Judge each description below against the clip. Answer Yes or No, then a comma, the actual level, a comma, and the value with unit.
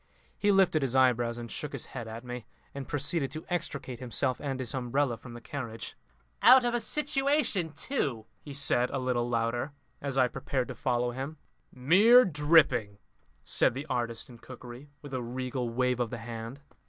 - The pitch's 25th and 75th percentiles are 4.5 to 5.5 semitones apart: No, average, 3.5 semitones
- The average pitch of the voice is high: No, low, 130 Hz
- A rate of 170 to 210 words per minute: Yes, average, 180 wpm